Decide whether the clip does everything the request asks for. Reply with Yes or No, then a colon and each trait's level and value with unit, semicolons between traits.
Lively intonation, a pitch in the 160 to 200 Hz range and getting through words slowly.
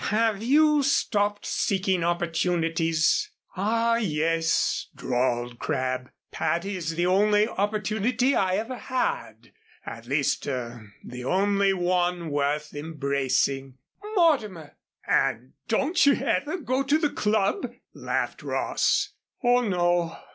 Yes: wide, 6.6 semitones; medium, 185 Hz; slow, 115 wpm